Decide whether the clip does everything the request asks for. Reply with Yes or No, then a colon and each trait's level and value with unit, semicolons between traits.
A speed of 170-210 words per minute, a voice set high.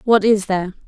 Yes: fast, 205 wpm; high, 205 Hz